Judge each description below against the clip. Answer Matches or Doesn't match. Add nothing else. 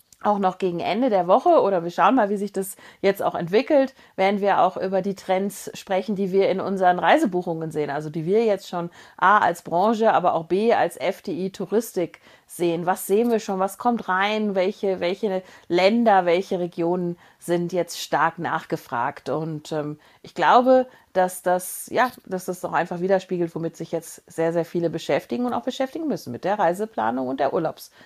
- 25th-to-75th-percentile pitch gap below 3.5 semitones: Matches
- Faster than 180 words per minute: Matches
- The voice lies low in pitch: Doesn't match